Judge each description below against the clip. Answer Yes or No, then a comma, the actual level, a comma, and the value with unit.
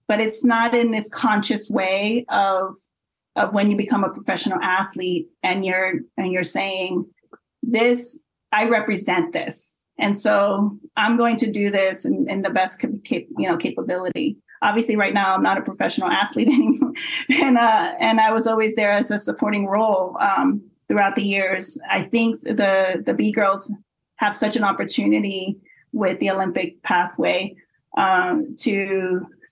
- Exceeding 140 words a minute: Yes, average, 160 wpm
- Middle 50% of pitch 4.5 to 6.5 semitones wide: No, average, 3.6 semitones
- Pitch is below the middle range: No, high, 210 Hz